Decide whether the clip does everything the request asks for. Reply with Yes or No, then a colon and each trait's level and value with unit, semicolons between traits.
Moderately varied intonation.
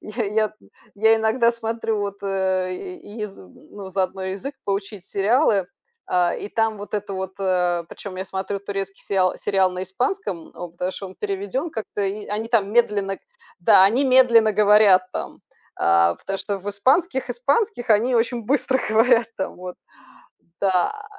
Yes: average, 3.2 semitones